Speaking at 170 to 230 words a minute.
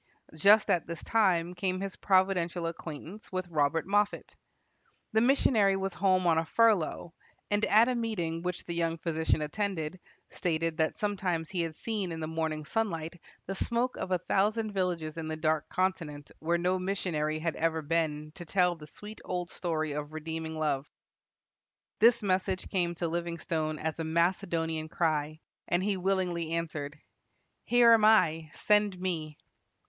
No: average, 160 wpm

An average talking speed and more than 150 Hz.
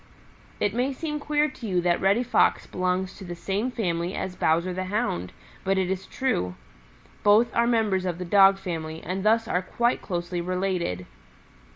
Yes: average, 180 wpm; high, 190 Hz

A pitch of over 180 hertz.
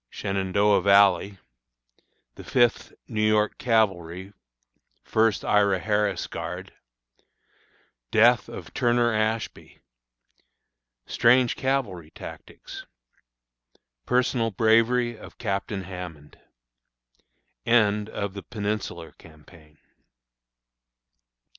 No: low, 105 Hz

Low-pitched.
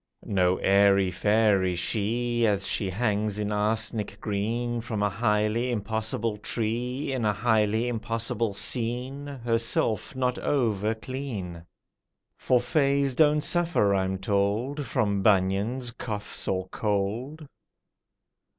Yes: low, 110 Hz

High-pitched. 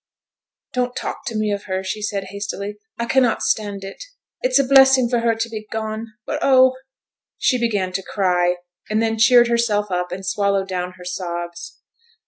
Yes: high, 210 Hz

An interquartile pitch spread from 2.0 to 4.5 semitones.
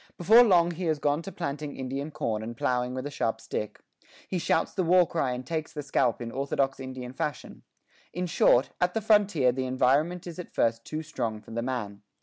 No: average, 5.2 semitones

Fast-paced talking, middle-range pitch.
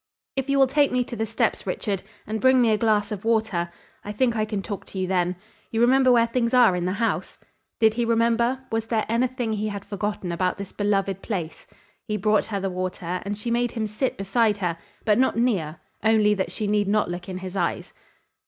No: fast, 225 wpm; high, 215 Hz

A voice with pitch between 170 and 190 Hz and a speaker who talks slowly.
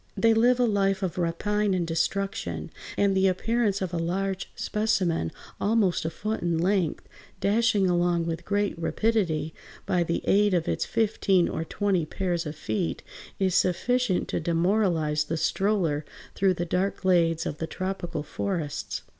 No: medium, 185 Hz; average, 155 wpm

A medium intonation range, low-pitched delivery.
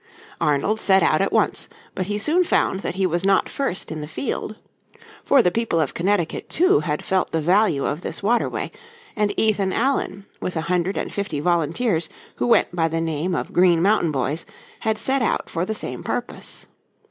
No: average, 4.6 semitones; medium, 185 Hz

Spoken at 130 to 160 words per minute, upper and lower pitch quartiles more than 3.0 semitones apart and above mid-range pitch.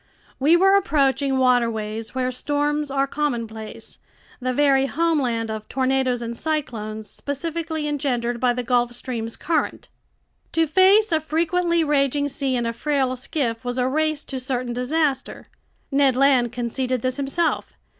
Yes: average, 145 wpm; average, 3.5 semitones; very high, 265 Hz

